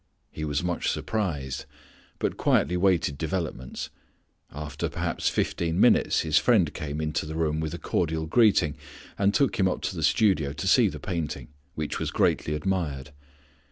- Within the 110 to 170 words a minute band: Yes, average, 160 wpm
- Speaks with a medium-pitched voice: No, very low, 80 Hz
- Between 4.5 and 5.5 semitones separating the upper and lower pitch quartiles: No, average, 3.6 semitones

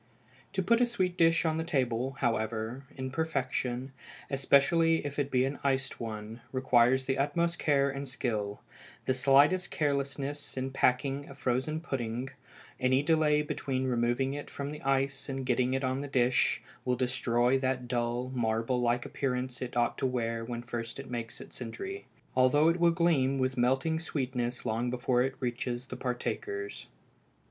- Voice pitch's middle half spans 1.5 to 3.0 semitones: Yes, narrow, 2.6 semitones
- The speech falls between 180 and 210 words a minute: No, average, 165 wpm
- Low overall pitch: Yes, low, 130 Hz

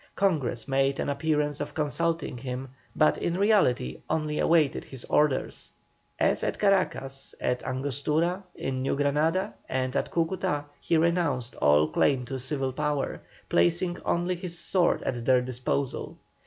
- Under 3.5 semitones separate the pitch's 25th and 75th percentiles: No, average, 4.3 semitones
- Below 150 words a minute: Yes, average, 140 wpm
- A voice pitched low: No, medium, 145 Hz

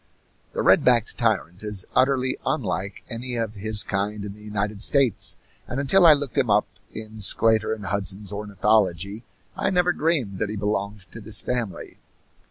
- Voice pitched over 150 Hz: No, low, 105 Hz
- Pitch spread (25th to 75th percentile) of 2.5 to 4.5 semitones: Yes, average, 3.4 semitones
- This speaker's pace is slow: No, average, 170 wpm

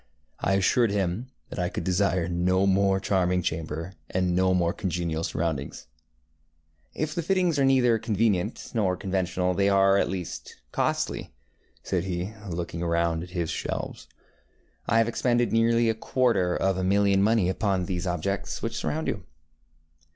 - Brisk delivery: No, average, 160 wpm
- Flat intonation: No, average, 3.8 semitones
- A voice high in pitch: No, very low, 95 Hz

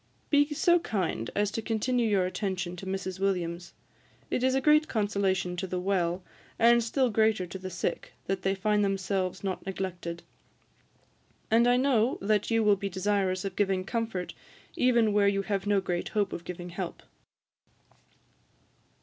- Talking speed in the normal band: Yes, average, 160 wpm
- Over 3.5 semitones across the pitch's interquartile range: No, average, 3.2 semitones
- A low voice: No, high, 195 Hz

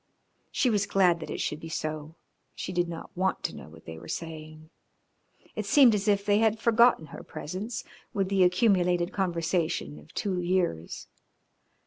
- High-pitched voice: No, medium, 180 Hz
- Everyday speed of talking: Yes, average, 170 wpm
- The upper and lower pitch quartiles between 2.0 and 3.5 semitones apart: No, average, 4.2 semitones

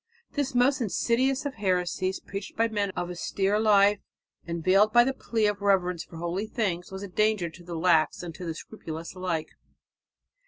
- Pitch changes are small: No, average, 3.7 semitones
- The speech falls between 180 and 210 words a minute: Yes, average, 185 wpm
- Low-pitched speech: No, high, 195 Hz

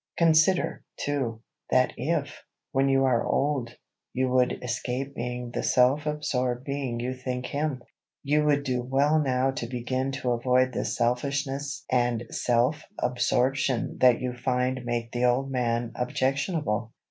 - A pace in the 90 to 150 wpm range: Yes, average, 145 wpm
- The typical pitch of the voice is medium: No, low, 130 Hz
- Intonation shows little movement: Yes, narrow, 2.1 semitones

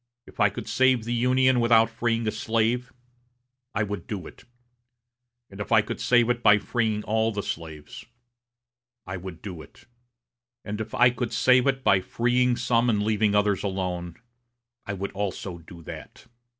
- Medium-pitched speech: No, low, 110 Hz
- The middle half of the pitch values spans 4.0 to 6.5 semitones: No, average, 3.4 semitones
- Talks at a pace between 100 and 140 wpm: No, average, 170 wpm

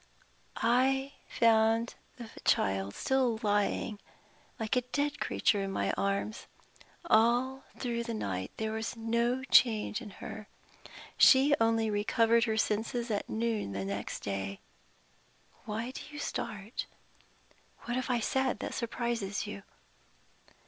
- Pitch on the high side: Yes, high, 225 Hz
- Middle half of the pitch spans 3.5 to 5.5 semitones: No, average, 2.8 semitones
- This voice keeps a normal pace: No, slow, 130 wpm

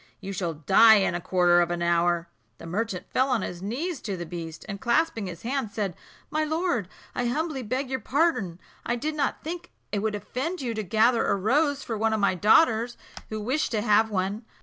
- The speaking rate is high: Yes, fast, 215 wpm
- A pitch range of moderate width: No, wide, 5.8 semitones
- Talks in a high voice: Yes, high, 220 Hz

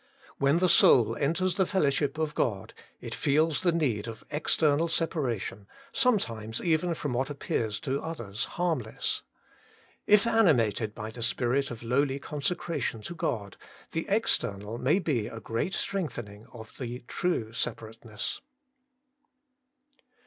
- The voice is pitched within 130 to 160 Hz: Yes, medium, 140 Hz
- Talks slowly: Yes, slow, 130 wpm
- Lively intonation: Yes, wide, 6.5 semitones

